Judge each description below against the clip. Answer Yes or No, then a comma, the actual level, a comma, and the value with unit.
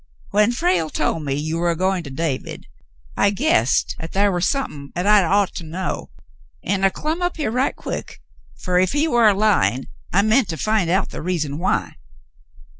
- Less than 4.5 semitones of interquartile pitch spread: No, average, 4.8 semitones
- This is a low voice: No, high, 190 Hz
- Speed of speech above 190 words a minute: Yes, average, 200 wpm